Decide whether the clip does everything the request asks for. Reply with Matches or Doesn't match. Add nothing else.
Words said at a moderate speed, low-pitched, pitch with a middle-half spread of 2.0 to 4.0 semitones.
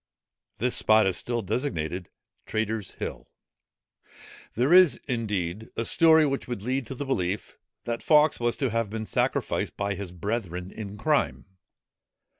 Doesn't match